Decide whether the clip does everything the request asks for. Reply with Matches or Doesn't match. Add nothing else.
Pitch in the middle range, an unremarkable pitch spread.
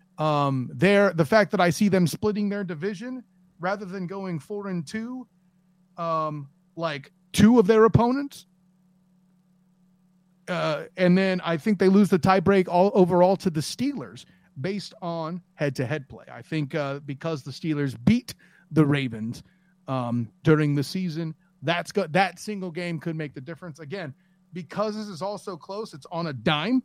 Matches